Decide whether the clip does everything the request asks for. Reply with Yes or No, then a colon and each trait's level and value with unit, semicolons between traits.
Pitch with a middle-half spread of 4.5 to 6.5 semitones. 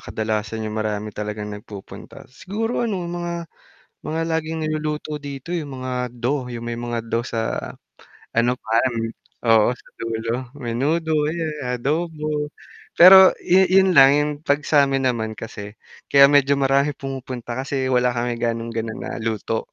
Yes: average, 4.9 semitones